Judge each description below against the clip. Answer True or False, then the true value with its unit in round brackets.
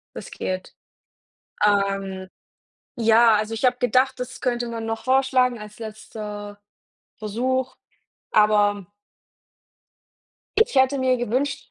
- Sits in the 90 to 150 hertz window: False (225 Hz)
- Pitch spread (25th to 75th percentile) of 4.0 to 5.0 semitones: False (3.5 semitones)